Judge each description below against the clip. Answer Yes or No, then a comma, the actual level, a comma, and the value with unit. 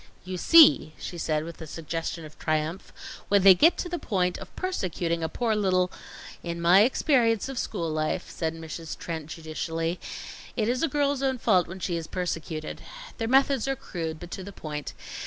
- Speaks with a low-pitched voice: No, medium, 180 Hz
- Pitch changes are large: Yes, wide, 5.9 semitones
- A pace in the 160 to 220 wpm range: Yes, average, 195 wpm